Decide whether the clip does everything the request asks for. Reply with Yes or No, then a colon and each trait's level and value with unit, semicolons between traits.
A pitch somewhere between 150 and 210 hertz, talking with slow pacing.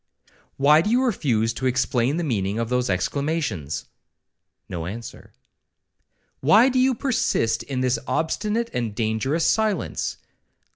No: low, 130 Hz; slow, 125 wpm